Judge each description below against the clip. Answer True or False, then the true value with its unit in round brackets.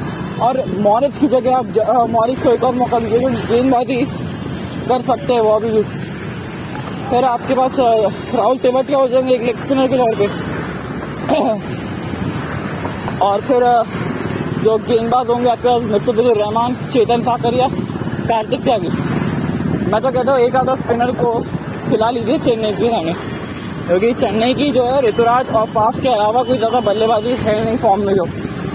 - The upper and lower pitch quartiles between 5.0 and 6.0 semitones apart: False (2.4 semitones)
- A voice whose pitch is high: True (240 Hz)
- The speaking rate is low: False (155 wpm)